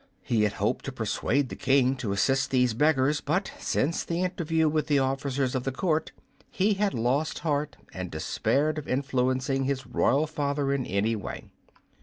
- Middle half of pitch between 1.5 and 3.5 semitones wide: Yes, average, 3.2 semitones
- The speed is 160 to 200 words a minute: Yes, average, 175 wpm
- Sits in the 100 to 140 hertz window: Yes, low, 135 Hz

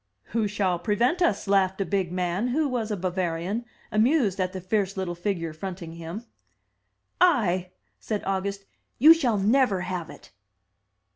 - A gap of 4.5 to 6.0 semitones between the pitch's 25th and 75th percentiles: No, average, 3.3 semitones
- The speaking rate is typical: Yes, average, 155 wpm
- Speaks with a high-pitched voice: Yes, high, 195 Hz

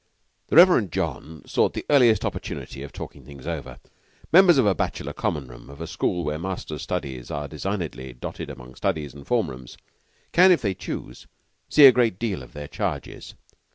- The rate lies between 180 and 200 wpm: Yes, average, 185 wpm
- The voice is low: Yes, very low, 80 Hz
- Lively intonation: Yes, wide, 8.7 semitones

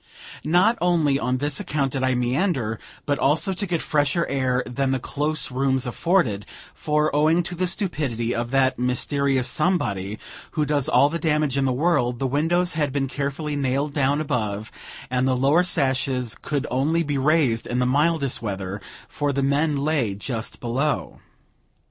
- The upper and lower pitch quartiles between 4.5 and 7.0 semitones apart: No, average, 3.4 semitones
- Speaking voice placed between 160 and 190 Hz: No, medium, 140 Hz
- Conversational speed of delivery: Yes, average, 170 wpm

